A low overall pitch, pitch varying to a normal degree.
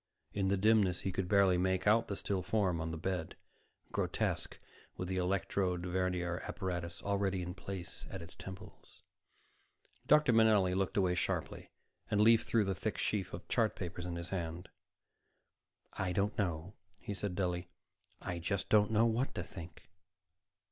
No: very low, 95 Hz; narrow, 2.2 semitones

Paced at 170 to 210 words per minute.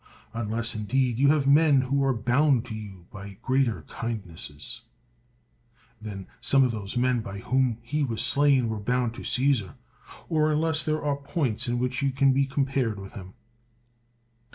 Yes: average, 175 wpm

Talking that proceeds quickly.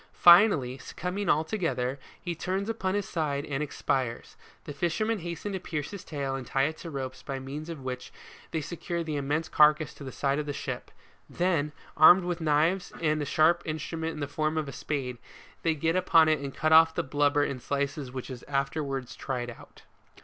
Yes: fast, 210 wpm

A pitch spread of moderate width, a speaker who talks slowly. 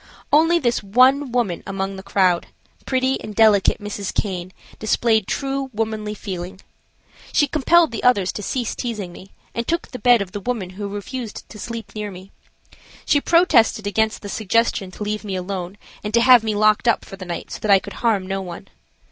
No: average, 3.8 semitones; average, 195 wpm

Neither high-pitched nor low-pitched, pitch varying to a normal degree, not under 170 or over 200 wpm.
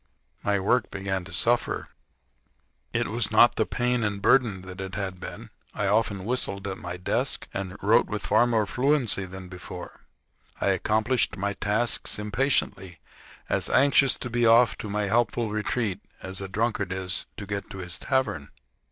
No: low, 100 Hz; average, 3.7 semitones; average, 175 wpm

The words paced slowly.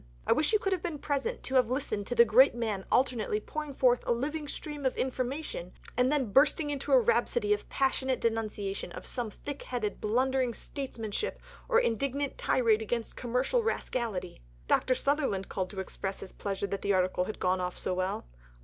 No: average, 185 wpm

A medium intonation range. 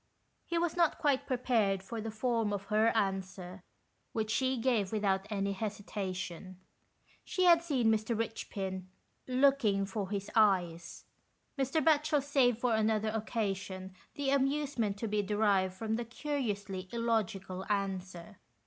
Yes: average, 4.4 semitones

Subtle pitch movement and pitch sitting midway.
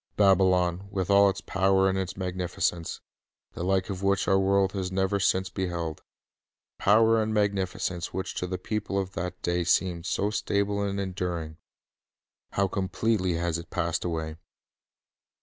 No: narrow, 1.9 semitones; very low, 95 Hz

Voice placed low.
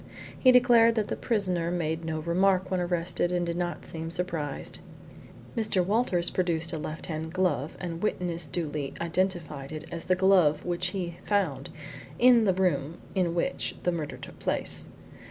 No: medium, 175 Hz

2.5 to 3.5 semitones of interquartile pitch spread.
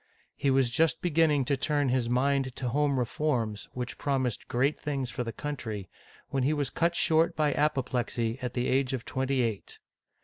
Yes: average, 3.1 semitones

